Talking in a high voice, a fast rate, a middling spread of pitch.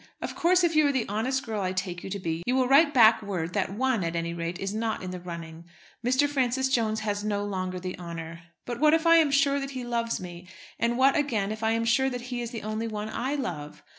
No: high, 220 Hz; fast, 260 wpm; wide, 6.1 semitones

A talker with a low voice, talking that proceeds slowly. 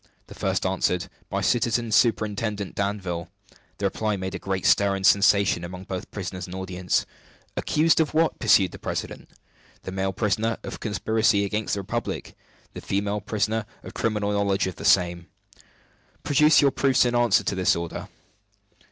No: low, 100 Hz; average, 160 wpm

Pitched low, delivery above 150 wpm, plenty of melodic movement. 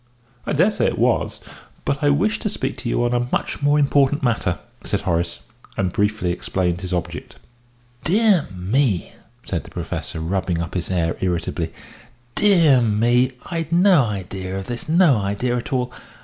Yes: low, 120 Hz; average, 165 wpm; wide, 7.7 semitones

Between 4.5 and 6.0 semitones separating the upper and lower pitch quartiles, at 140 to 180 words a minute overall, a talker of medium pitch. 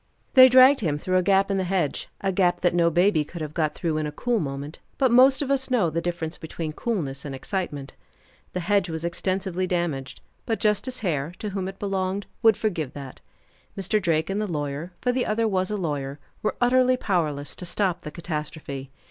No: average, 5.1 semitones; fast, 205 wpm; medium, 180 Hz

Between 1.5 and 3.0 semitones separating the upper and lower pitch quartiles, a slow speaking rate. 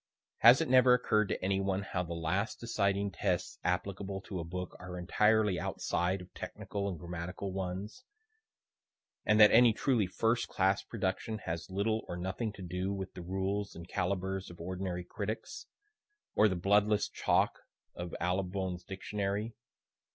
No: narrow, 2.6 semitones; average, 155 wpm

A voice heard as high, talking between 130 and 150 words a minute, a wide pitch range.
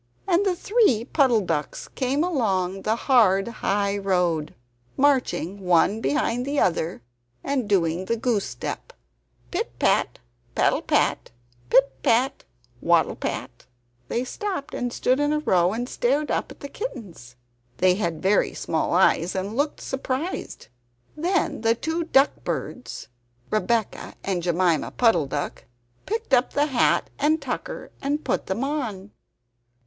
Yes: high, 230 Hz; average, 140 wpm; wide, 7.1 semitones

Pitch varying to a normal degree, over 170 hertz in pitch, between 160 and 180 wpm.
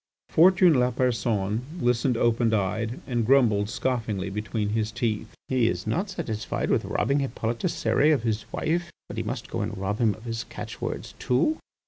No: average, 3.4 semitones; low, 115 Hz; average, 165 wpm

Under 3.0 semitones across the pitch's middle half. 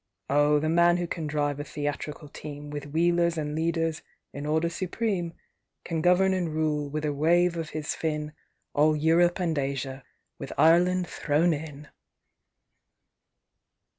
Yes: narrow, 2.5 semitones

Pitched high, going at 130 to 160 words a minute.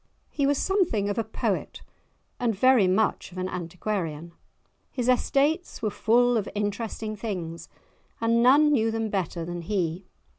Yes: high, 215 Hz; average, 150 wpm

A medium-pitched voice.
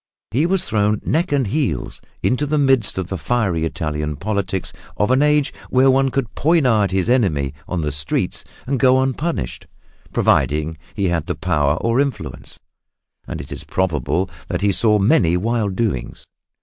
No: low, 105 Hz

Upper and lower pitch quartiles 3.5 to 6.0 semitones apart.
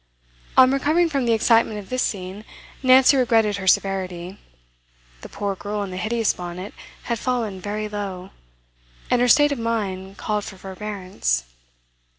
Yes: average, 3.8 semitones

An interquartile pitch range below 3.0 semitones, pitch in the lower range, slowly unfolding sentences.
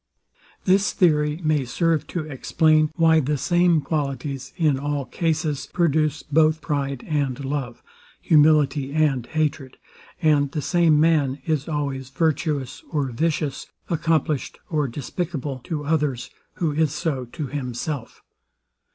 No: narrow, 2.5 semitones; medium, 150 Hz; slow, 125 wpm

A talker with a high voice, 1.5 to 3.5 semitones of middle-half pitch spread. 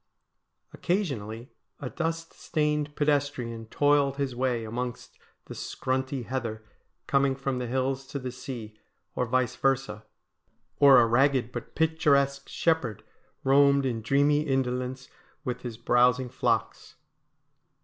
No: low, 130 Hz; narrow, 2.5 semitones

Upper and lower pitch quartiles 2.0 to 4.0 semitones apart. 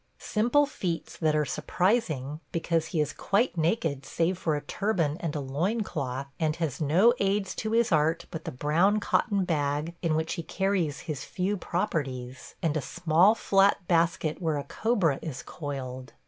No: average, 4.7 semitones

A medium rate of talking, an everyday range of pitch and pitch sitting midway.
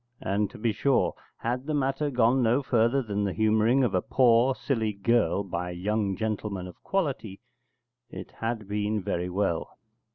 No: average, 170 wpm; average, 3.8 semitones; low, 110 Hz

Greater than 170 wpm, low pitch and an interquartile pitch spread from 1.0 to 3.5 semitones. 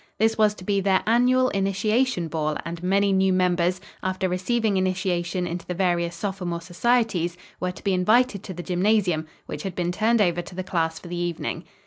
No: average, 190 wpm; medium, 185 Hz; average, 2.8 semitones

